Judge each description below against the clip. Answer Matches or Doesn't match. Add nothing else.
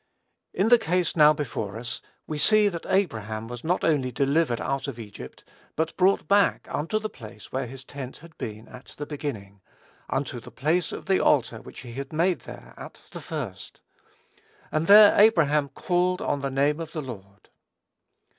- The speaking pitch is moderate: Matches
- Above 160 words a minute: Matches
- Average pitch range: Doesn't match